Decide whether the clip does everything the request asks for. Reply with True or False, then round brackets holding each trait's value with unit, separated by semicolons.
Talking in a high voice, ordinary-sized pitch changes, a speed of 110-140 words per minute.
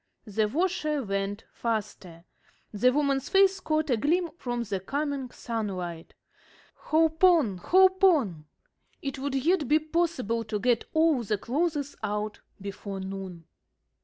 False (255 Hz; 7.4 semitones; 135 wpm)